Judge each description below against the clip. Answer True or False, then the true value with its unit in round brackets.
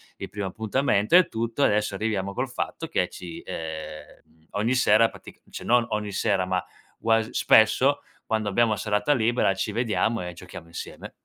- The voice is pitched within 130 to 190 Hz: False (110 Hz)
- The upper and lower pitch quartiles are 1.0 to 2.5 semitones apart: False (2.9 semitones)